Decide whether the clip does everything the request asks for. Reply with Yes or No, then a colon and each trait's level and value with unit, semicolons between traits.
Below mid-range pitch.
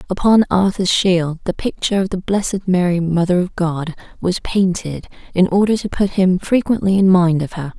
No: medium, 185 Hz